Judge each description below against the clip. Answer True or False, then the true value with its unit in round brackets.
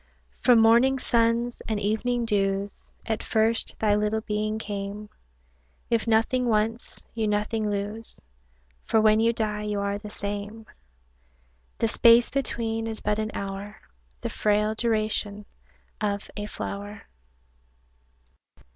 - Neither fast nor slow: False (125 wpm)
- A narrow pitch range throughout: True (1.6 semitones)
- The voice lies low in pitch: False (215 Hz)